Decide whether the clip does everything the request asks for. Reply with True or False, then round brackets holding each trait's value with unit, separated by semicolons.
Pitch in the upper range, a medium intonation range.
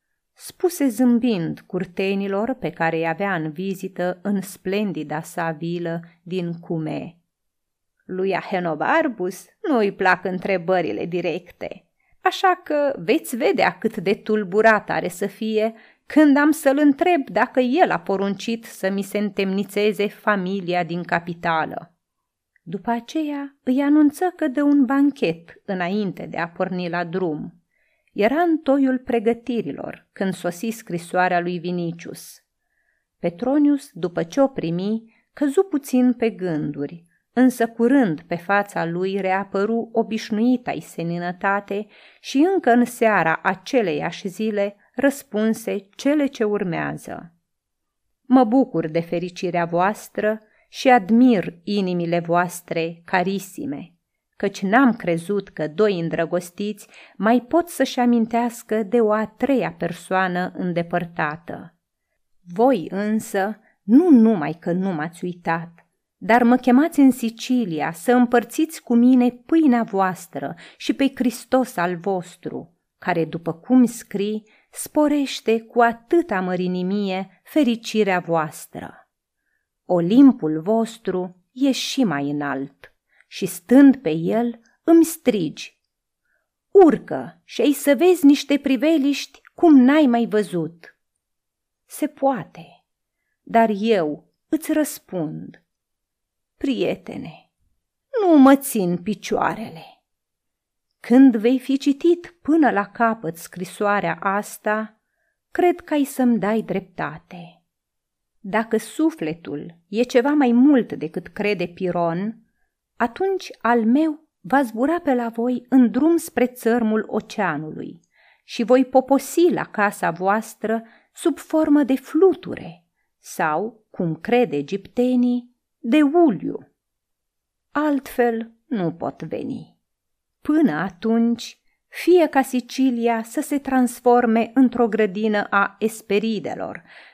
False (220 Hz; 6.2 semitones)